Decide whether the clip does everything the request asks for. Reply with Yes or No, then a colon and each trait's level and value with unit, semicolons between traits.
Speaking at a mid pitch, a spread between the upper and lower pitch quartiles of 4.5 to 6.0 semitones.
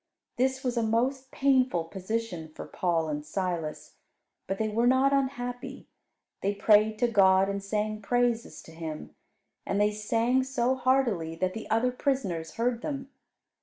No: high, 225 Hz; average, 4.9 semitones